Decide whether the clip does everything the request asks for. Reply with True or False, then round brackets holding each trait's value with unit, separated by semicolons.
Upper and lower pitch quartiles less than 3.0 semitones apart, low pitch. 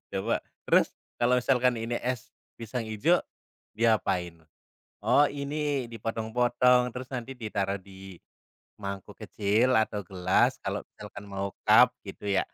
False (4.0 semitones; 115 Hz)